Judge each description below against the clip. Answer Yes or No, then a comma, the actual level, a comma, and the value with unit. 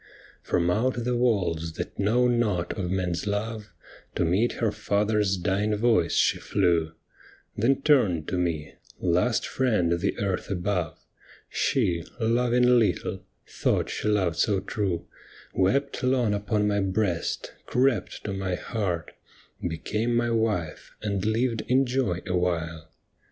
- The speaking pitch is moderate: No, low, 105 Hz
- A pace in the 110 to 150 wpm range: Yes, average, 140 wpm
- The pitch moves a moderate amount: Yes, average, 4.7 semitones